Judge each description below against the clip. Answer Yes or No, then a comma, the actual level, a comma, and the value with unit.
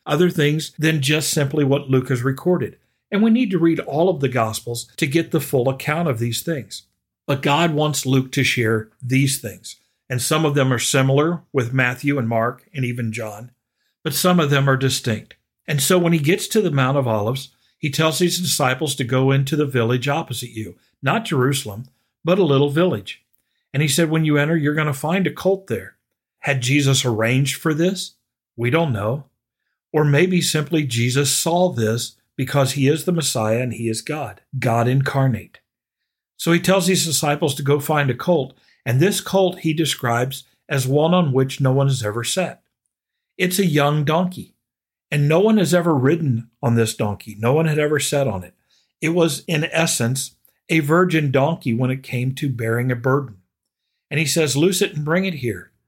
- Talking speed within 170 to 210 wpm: Yes, average, 200 wpm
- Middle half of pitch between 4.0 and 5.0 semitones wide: Yes, average, 4.5 semitones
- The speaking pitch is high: No, medium, 140 Hz